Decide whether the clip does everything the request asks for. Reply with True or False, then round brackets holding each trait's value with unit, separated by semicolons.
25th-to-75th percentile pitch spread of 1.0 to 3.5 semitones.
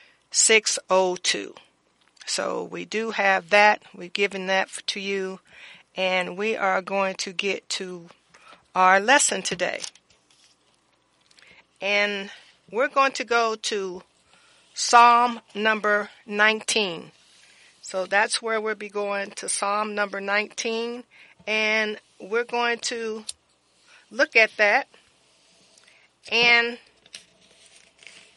True (2.4 semitones)